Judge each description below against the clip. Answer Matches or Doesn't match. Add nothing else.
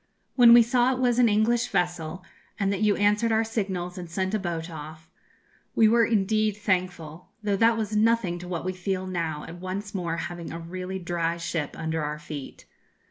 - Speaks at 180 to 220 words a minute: Matches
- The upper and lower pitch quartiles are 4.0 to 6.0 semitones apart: Matches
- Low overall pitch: Doesn't match